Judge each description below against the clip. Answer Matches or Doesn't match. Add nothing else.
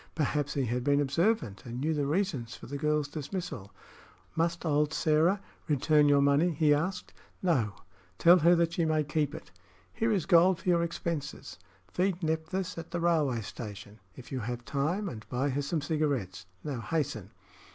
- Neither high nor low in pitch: Matches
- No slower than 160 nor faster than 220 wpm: Matches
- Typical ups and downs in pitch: Matches